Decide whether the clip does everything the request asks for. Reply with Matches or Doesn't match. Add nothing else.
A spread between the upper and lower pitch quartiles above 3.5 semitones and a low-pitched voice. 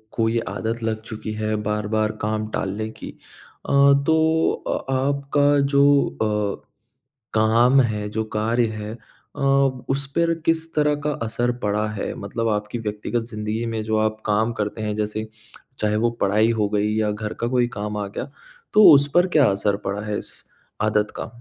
Doesn't match